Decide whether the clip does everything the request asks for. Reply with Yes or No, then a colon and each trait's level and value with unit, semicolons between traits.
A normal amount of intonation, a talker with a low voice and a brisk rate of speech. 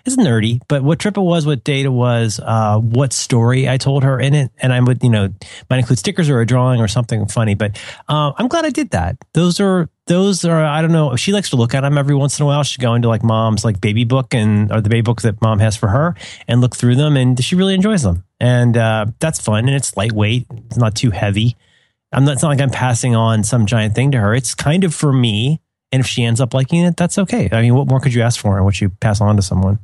Yes: average, 4.4 semitones; low, 125 Hz; fast, 275 wpm